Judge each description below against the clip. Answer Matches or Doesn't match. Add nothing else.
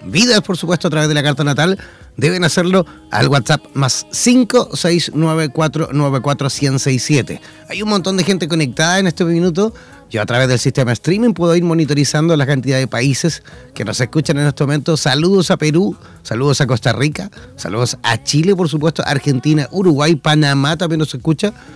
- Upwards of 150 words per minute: Matches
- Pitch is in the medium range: Matches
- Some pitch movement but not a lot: Matches